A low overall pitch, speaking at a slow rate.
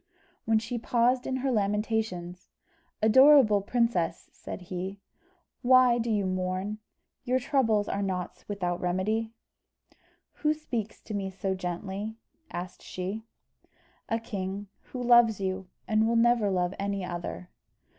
No: high, 210 Hz; slow, 130 wpm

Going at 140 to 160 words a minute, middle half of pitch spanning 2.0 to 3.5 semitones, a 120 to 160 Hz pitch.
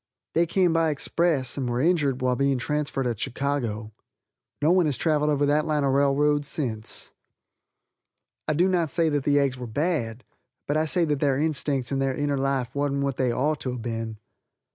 No: average, 195 wpm; average, 2.9 semitones; medium, 140 Hz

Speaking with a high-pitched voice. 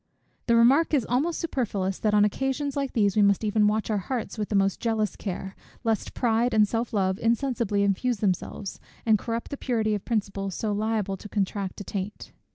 Yes: high, 215 Hz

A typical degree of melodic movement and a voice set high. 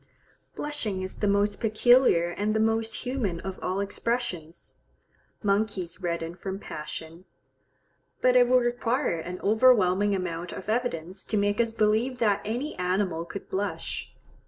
Yes: average, 4.2 semitones; high, 205 Hz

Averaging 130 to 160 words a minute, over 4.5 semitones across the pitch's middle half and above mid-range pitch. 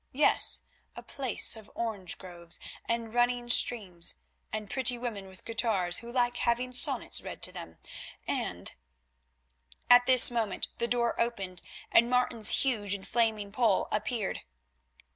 No: average, 140 wpm; average, 3.3 semitones; high, 230 Hz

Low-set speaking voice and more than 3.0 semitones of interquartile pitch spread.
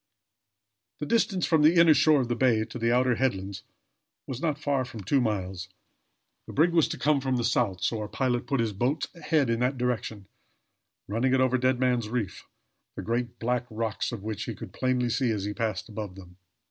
Yes: low, 120 Hz; average, 3.4 semitones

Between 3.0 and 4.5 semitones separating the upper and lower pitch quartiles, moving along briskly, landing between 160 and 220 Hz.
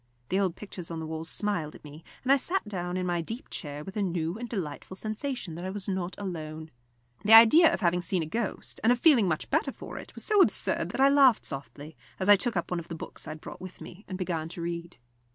No: average, 5.0 semitones; fast, 260 wpm; medium, 185 Hz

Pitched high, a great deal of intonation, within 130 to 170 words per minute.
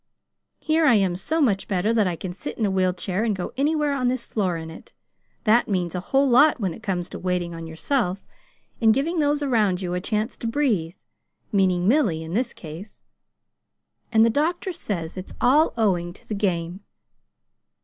No: high, 205 Hz; wide, 6.1 semitones; average, 195 wpm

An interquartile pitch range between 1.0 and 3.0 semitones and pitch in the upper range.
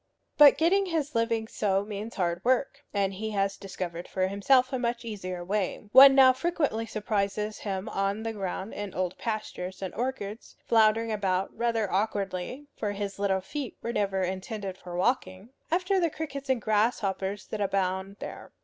No: average, 3.8 semitones; high, 210 Hz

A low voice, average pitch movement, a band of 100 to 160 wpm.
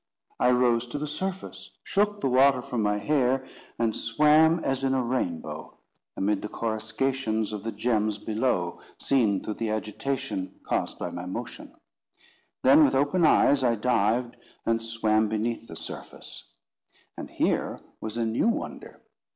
Yes: low, 115 Hz; average, 3.7 semitones; average, 150 wpm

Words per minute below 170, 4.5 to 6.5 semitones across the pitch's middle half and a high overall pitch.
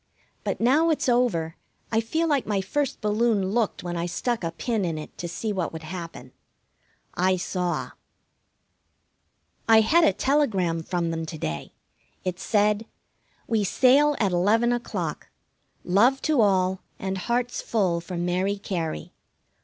Yes: average, 150 wpm; average, 5.3 semitones; high, 200 Hz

